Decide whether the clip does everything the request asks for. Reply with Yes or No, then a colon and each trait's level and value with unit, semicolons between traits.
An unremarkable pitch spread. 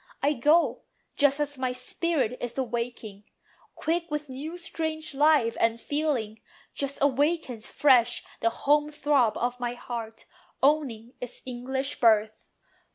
Yes: average, 3.9 semitones